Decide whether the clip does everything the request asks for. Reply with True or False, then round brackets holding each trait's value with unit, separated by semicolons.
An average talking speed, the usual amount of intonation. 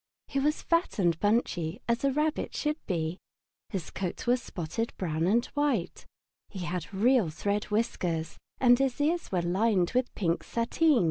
False (160 wpm; 6.8 semitones)